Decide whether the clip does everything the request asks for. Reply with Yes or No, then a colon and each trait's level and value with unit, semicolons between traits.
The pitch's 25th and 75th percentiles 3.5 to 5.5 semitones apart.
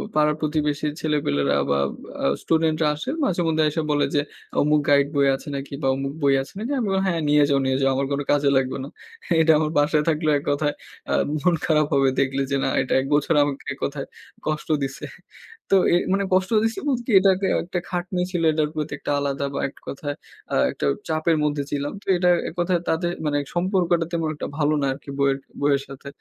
No: average, 3.0 semitones